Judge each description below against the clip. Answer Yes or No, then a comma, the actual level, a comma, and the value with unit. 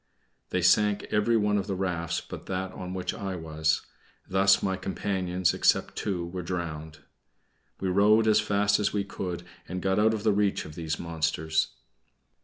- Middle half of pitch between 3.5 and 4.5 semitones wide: No, average, 3.1 semitones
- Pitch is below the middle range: Yes, very low, 95 Hz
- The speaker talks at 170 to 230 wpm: Yes, average, 180 wpm